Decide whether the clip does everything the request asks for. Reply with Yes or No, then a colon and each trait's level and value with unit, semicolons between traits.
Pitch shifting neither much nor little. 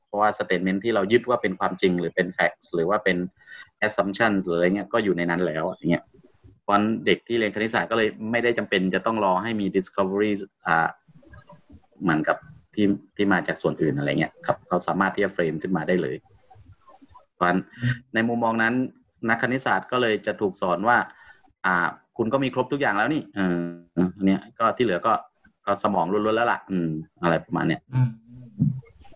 Yes: average, 4.1 semitones